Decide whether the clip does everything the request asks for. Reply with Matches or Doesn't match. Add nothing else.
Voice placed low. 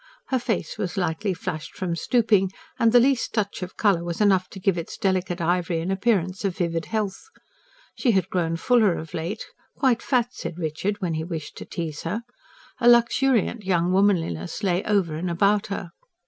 Doesn't match